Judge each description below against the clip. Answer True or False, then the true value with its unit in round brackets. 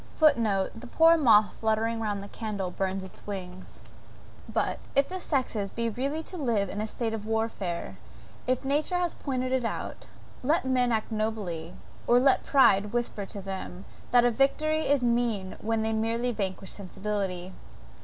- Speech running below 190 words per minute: True (165 wpm)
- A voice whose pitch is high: True (225 Hz)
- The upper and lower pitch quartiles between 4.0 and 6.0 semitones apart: True (4.3 semitones)